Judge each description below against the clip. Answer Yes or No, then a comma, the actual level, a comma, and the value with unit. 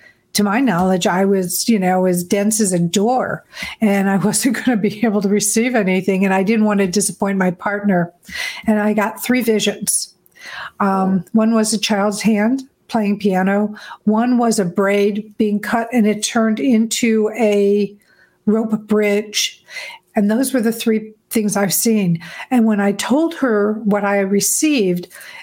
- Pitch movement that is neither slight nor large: No, narrow, 2.1 semitones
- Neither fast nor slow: Yes, average, 170 wpm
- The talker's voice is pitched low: No, high, 210 Hz